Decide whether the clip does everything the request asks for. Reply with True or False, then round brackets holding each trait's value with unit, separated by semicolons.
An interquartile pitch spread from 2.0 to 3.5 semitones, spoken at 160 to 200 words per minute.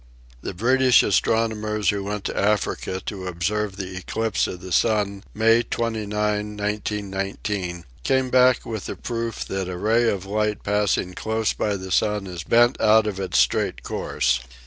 True (2.4 semitones; 165 wpm)